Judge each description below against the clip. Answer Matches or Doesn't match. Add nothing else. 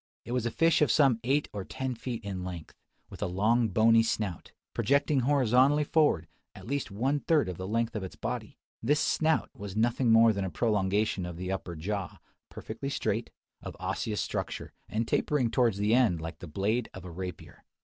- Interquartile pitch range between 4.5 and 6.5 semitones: Matches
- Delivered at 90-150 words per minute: Doesn't match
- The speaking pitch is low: Matches